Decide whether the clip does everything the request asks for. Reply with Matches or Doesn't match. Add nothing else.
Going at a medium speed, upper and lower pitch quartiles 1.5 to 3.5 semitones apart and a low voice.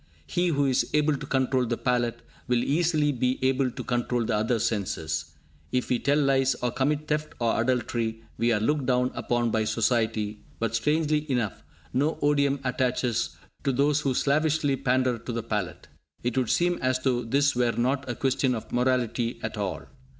Matches